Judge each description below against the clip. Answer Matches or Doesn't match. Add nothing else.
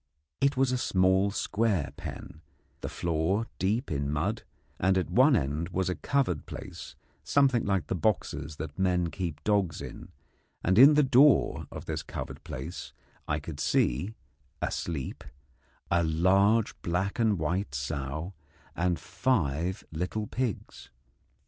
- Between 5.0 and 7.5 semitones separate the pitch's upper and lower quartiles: Matches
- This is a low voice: Matches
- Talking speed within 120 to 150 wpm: Matches